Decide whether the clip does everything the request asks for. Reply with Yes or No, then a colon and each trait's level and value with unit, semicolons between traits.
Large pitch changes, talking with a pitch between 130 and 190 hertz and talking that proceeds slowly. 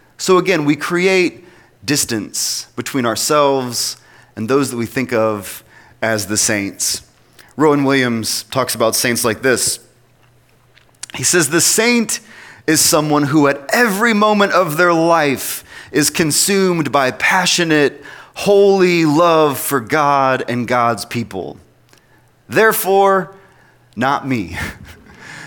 Yes: wide, 6.8 semitones; medium, 140 Hz; slow, 120 wpm